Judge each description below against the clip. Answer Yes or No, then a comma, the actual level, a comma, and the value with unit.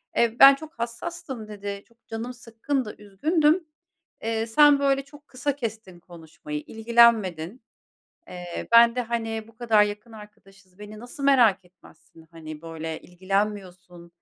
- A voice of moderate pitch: No, high, 220 Hz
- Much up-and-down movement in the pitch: No, average, 4.6 semitones